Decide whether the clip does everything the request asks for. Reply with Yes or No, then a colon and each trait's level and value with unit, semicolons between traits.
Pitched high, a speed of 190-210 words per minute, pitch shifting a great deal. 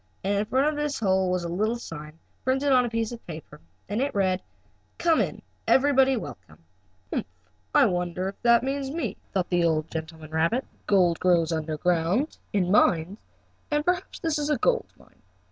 Yes: high, 200 Hz; average, 195 wpm; wide, 7.9 semitones